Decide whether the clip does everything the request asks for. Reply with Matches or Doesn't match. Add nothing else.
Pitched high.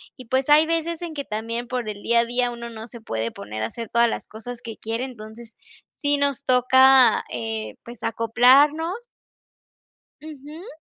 Matches